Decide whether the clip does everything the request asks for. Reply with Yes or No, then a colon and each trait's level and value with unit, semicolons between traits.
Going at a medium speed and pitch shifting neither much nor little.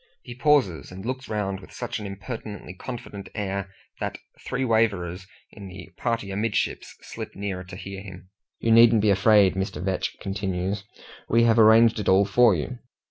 Yes: average, 170 wpm; average, 3.1 semitones